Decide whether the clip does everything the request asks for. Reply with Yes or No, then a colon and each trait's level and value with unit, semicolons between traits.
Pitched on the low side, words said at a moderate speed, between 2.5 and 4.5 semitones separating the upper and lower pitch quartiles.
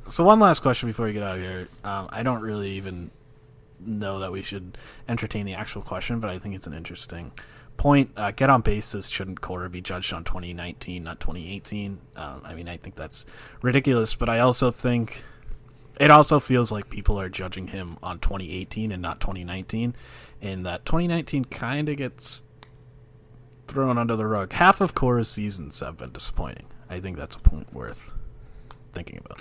No: low, 105 Hz; average, 185 wpm; average, 5.1 semitones